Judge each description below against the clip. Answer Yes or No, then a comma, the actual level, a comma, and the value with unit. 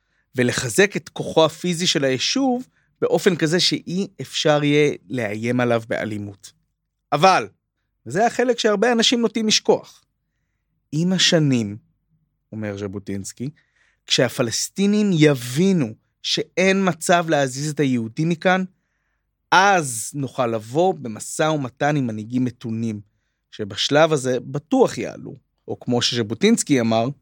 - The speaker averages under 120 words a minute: Yes, average, 110 wpm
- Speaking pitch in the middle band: Yes, medium, 145 Hz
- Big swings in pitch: Yes, wide, 7.0 semitones